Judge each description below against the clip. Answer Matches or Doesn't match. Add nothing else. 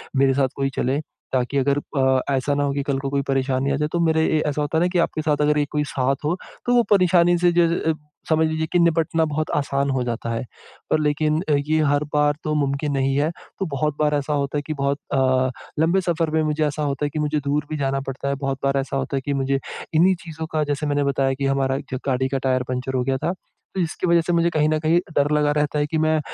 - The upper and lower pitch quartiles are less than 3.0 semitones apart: Matches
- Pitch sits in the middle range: Matches